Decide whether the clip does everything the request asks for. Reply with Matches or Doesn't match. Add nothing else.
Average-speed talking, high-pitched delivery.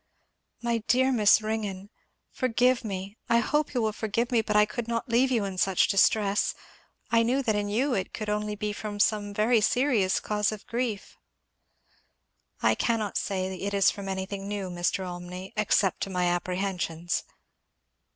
Matches